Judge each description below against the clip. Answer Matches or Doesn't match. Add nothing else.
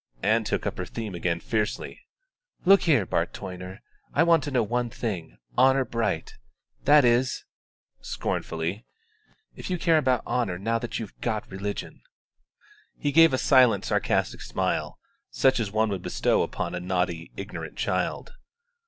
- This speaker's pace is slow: Doesn't match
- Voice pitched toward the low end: Matches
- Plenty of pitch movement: Matches